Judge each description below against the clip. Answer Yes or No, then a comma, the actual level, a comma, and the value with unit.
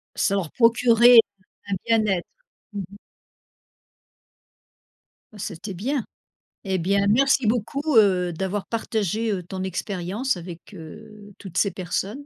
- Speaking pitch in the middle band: No, high, 200 Hz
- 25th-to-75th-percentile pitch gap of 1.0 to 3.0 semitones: No, average, 3.5 semitones